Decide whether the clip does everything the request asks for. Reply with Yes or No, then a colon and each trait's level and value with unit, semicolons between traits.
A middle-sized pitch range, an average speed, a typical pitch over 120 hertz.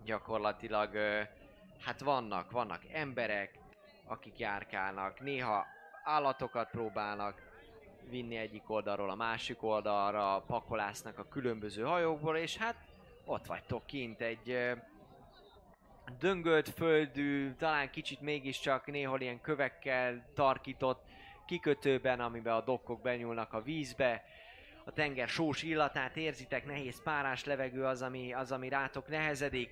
Yes: average, 4.2 semitones; average, 115 wpm; low, 130 Hz